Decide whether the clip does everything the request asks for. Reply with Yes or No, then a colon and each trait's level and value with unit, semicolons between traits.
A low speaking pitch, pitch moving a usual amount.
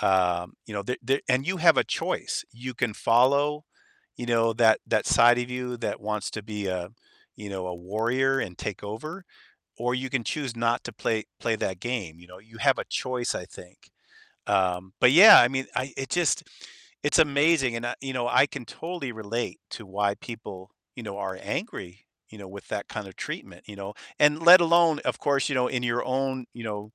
Yes: low, 120 Hz; average, 4.7 semitones